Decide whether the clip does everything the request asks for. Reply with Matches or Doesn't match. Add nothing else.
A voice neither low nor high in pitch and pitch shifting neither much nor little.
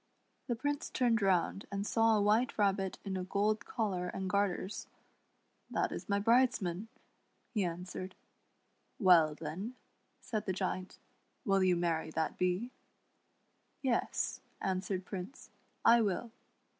Doesn't match